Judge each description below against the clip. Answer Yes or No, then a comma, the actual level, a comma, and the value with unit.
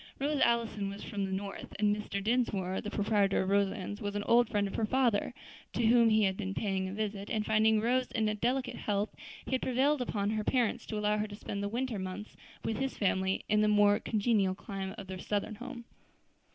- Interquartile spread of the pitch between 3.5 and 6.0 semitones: No, average, 2.7 semitones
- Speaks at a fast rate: Yes, fast, 220 wpm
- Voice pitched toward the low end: No, high, 210 Hz